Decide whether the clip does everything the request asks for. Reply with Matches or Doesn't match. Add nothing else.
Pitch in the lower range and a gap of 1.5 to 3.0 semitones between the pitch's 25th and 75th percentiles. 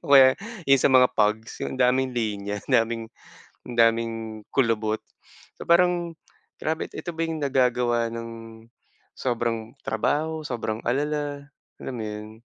Doesn't match